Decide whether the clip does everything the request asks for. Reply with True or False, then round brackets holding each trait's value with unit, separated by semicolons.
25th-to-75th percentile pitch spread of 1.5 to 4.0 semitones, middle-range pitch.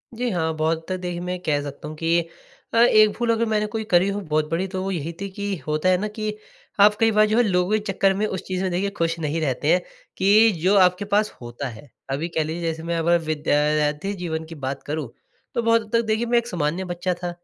False (4.6 semitones; 180 Hz)